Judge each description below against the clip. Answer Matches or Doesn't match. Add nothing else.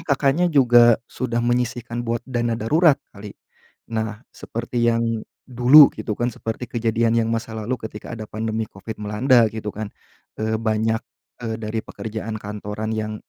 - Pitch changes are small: Matches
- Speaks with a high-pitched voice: Doesn't match